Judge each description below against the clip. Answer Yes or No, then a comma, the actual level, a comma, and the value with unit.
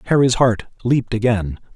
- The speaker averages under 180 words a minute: Yes, slow, 135 wpm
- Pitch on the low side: Yes, low, 115 Hz